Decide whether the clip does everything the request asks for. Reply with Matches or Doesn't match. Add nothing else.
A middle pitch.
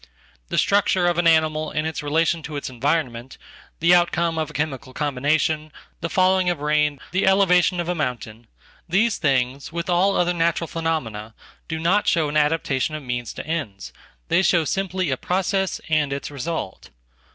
Matches